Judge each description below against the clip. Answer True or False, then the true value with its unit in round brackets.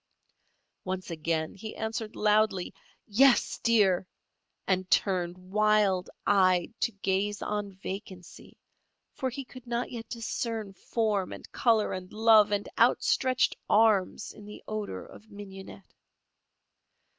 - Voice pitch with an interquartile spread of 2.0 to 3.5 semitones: True (2.8 semitones)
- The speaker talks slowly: True (120 wpm)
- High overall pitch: True (205 Hz)